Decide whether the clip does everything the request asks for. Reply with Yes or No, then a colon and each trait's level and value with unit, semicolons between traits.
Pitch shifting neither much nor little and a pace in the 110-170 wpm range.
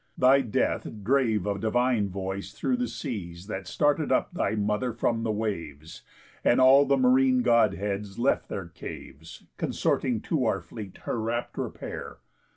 Yes: average, 4.6 semitones; average, 155 wpm